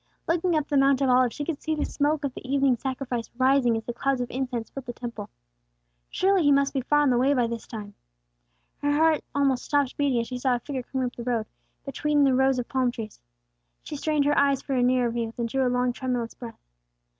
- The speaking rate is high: Yes, fast, 240 wpm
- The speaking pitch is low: No, very high, 260 Hz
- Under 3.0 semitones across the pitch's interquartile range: Yes, narrow, 2.6 semitones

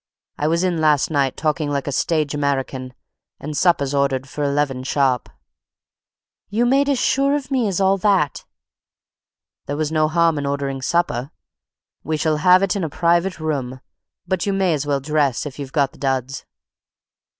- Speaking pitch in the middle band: Yes, medium, 150 Hz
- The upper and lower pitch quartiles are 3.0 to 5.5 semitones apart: Yes, average, 3.9 semitones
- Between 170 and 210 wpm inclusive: Yes, average, 175 wpm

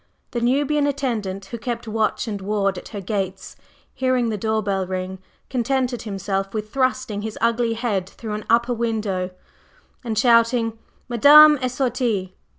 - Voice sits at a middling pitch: No, high, 225 Hz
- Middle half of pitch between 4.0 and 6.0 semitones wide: No, average, 3.6 semitones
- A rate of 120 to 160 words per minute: Yes, average, 155 wpm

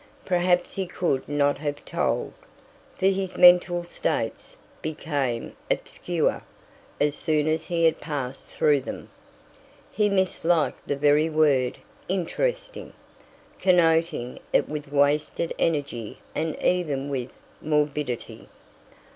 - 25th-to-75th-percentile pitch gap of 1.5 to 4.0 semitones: Yes, average, 3.6 semitones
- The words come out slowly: Yes, slow, 110 wpm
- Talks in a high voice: No, medium, 155 Hz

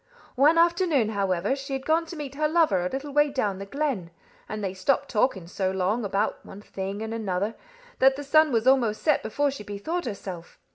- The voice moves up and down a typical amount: No, wide, 6.5 semitones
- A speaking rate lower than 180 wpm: No, fast, 205 wpm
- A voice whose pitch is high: Yes, high, 235 Hz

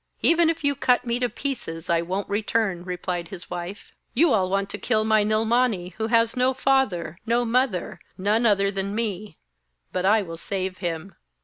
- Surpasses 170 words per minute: Yes, average, 185 wpm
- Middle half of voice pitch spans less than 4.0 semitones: No, average, 4.5 semitones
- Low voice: No, high, 205 Hz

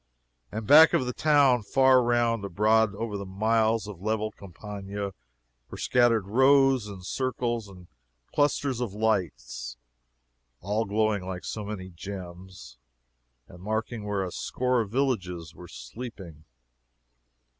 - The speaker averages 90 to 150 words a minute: Yes, slow, 135 wpm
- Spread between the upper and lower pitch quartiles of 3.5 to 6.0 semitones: Yes, average, 4.0 semitones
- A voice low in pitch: Yes, low, 105 Hz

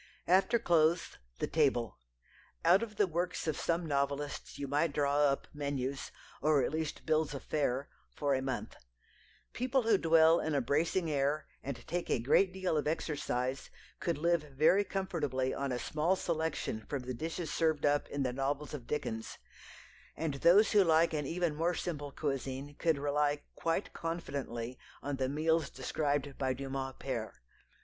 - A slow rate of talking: No, average, 165 wpm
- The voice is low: No, medium, 150 Hz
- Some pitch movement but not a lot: Yes, average, 3.3 semitones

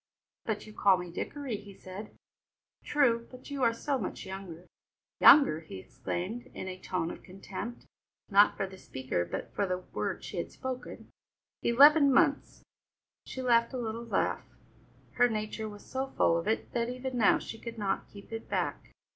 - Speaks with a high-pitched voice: Yes, high, 220 Hz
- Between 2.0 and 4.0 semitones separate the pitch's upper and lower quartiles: No, average, 4.6 semitones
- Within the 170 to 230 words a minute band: Yes, average, 175 wpm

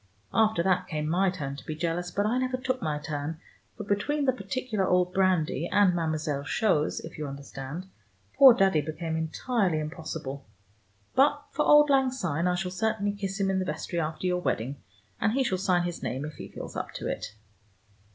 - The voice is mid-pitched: Yes, medium, 180 Hz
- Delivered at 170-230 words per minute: Yes, average, 195 wpm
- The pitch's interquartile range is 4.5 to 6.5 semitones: Yes, average, 5.0 semitones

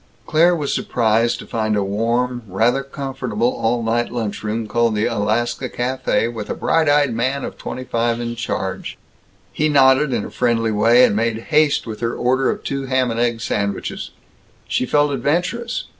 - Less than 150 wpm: No, average, 180 wpm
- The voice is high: No, low, 120 Hz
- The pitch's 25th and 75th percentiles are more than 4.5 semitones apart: No, average, 2.9 semitones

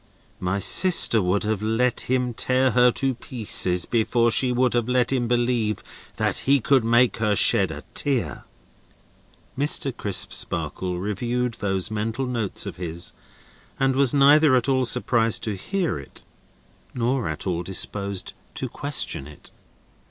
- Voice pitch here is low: Yes, low, 120 Hz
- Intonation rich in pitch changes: No, average, 4.1 semitones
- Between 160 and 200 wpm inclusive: No, average, 145 wpm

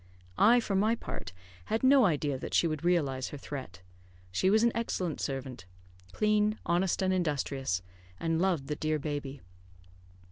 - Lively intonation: Yes, wide, 6.2 semitones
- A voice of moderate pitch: Yes, medium, 160 Hz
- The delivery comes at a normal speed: Yes, average, 155 wpm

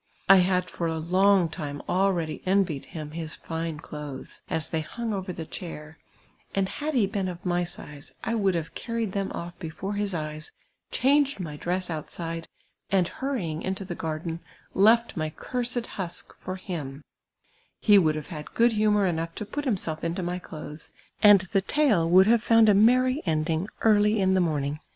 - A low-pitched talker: No, medium, 180 Hz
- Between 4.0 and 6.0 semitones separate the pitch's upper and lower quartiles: Yes, average, 4.3 semitones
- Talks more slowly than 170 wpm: No, average, 185 wpm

